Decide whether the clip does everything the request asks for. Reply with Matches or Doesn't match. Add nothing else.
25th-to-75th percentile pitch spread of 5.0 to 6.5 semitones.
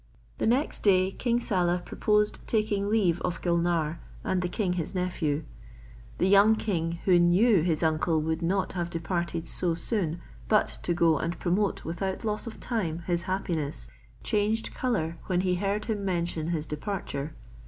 Doesn't match